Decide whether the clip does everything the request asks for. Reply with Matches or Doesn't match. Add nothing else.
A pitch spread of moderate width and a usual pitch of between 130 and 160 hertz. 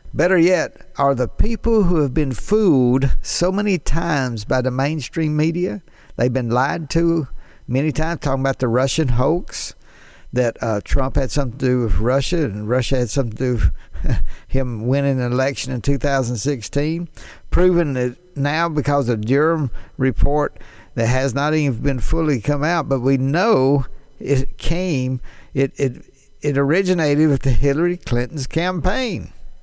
Matches